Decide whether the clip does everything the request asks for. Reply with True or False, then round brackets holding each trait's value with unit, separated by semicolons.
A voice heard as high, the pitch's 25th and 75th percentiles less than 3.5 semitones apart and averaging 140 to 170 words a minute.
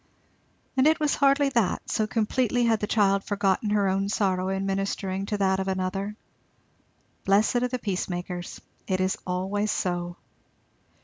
True (195 Hz; 2.6 semitones; 150 wpm)